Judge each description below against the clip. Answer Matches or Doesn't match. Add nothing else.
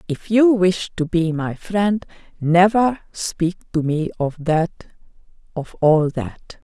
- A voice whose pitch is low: Doesn't match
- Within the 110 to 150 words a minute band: Matches